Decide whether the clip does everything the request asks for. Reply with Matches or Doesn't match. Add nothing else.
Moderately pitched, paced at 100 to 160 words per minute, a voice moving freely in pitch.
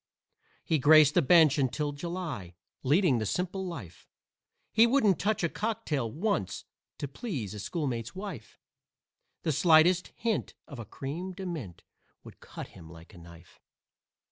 Matches